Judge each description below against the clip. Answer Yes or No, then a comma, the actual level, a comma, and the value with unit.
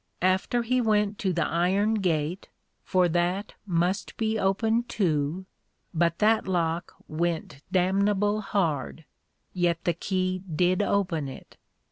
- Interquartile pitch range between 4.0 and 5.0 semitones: No, average, 3.4 semitones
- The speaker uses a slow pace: Yes, slow, 125 wpm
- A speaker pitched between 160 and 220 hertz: Yes, medium, 185 Hz